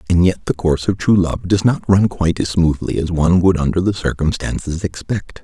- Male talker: Yes, male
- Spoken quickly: Yes, fast, 220 wpm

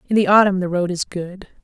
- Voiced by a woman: Yes, female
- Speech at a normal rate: No, fast, 255 wpm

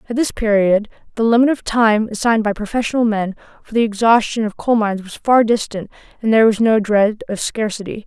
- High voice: Yes, high, 220 Hz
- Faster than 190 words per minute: Yes, average, 200 wpm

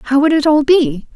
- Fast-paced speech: Yes, fast, 260 wpm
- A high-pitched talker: Yes, very high, 290 Hz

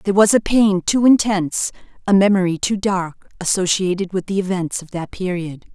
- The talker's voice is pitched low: No, high, 190 Hz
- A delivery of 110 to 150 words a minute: No, average, 180 wpm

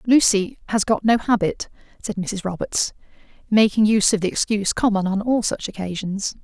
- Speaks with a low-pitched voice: No, high, 210 Hz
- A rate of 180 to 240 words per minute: No, average, 170 wpm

